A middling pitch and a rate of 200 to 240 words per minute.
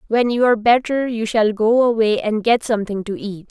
No: high, 225 Hz; fast, 205 wpm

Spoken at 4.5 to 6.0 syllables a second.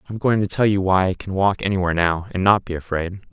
No: 6.5 syllables/s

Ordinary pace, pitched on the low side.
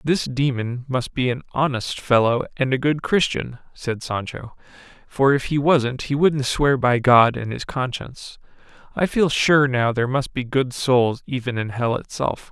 Yes: average, 180 wpm; low, 130 Hz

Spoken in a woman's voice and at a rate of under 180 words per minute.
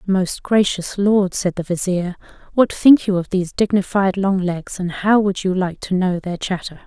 No: female; average, 200 wpm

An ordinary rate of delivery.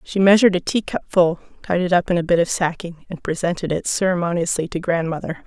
No: fast, 210 wpm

